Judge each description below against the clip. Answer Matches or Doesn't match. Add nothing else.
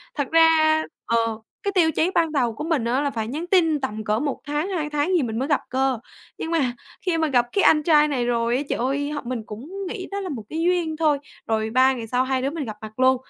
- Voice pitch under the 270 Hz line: Doesn't match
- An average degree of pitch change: Matches